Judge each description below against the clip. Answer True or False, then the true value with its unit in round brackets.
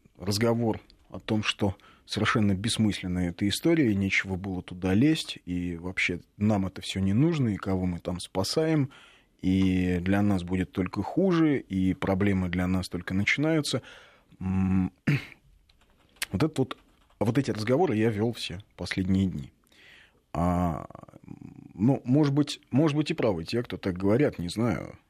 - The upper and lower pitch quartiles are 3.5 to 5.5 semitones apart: True (4.3 semitones)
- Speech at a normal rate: True (150 wpm)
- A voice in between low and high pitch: False (100 Hz)